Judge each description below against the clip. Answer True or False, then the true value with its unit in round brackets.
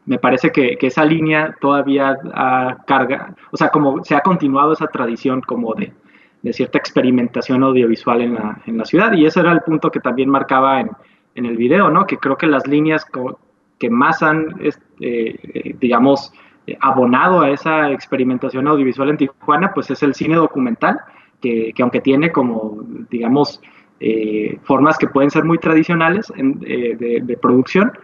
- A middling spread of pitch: True (3.6 semitones)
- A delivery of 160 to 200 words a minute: True (175 wpm)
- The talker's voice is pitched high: False (140 Hz)